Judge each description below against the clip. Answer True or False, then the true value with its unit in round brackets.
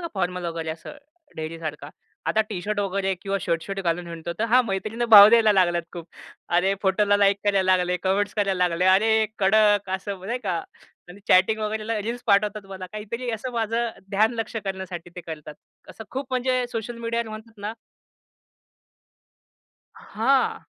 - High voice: True (200 Hz)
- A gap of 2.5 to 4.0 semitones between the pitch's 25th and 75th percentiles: True (3.4 semitones)